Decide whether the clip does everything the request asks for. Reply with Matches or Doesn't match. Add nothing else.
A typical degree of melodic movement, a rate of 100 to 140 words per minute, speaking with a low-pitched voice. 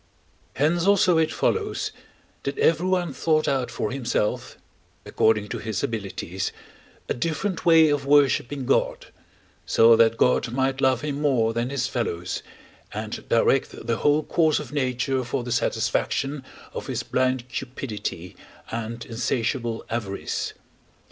Matches